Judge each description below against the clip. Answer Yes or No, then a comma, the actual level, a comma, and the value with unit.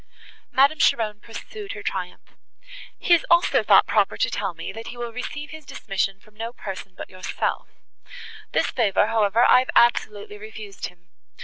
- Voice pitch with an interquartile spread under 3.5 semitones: No, average, 4.1 semitones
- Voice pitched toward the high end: Yes, high, 220 Hz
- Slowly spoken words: No, average, 170 wpm